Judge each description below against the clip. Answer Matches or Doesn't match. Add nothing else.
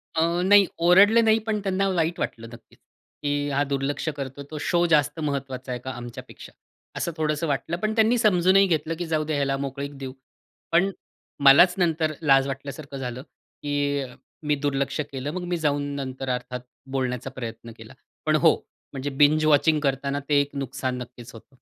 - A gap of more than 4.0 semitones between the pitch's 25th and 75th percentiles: Doesn't match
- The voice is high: Doesn't match